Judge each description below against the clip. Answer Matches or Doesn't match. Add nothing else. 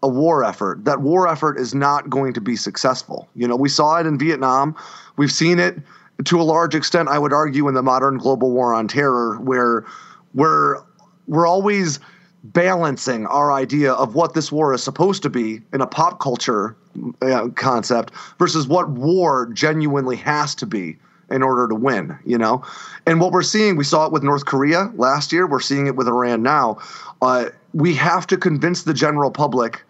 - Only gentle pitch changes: Doesn't match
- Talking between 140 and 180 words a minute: Doesn't match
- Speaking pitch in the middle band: Matches